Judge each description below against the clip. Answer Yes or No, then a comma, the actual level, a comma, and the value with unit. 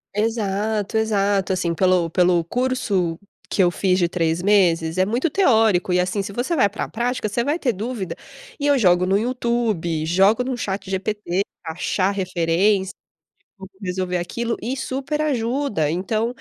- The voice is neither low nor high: No, high, 200 Hz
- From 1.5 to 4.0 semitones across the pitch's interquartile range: No, average, 4.5 semitones